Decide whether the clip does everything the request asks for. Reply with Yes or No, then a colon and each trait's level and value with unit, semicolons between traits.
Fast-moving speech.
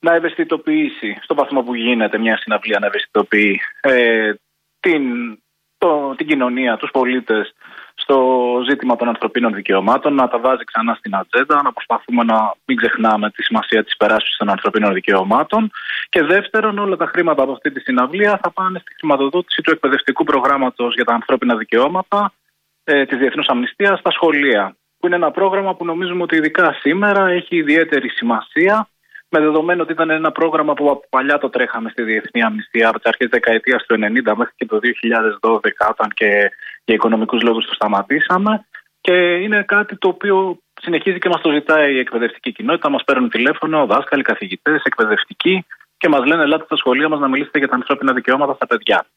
Yes: fast, 175 wpm